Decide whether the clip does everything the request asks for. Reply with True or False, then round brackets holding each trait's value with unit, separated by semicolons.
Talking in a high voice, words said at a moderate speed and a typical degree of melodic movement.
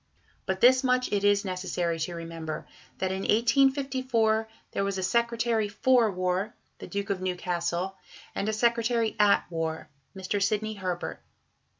True (200 Hz; 150 wpm; 4.1 semitones)